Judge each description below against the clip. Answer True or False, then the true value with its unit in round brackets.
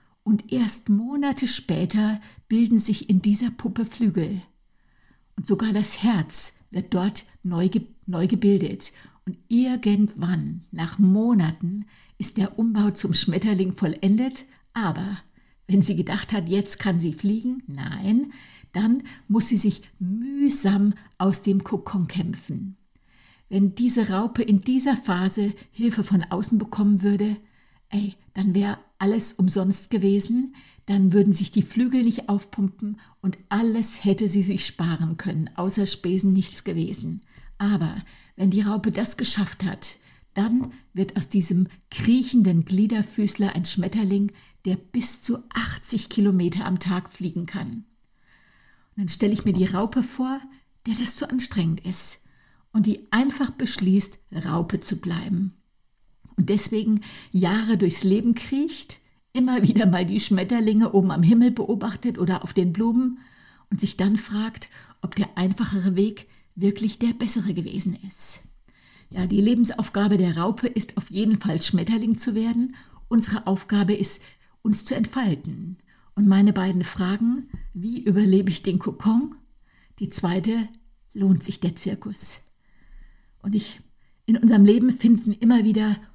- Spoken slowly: False (140 wpm)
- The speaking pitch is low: False (205 Hz)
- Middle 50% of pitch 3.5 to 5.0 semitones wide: False (2.8 semitones)